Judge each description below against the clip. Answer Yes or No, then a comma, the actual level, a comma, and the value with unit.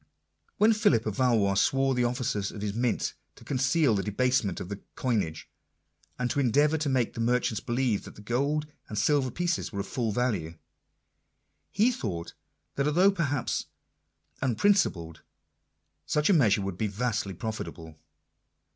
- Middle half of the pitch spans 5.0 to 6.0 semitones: Yes, wide, 5.4 semitones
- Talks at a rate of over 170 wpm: No, average, 155 wpm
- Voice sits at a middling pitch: No, low, 120 Hz